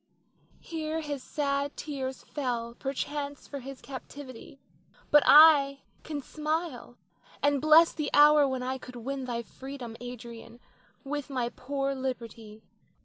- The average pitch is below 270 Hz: No, very high, 275 Hz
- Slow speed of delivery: Yes, slow, 130 wpm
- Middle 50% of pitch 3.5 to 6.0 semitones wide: No, average, 2.7 semitones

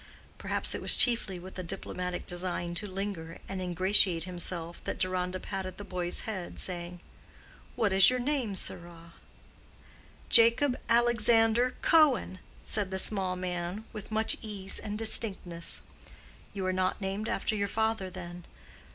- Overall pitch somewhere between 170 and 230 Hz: Yes, high, 190 Hz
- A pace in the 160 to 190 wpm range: No, average, 145 wpm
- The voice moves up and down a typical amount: Yes, average, 3.5 semitones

